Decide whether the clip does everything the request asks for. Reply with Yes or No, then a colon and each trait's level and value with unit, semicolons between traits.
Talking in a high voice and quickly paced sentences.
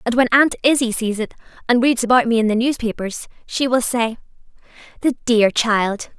No: high, 235 Hz; average, 185 wpm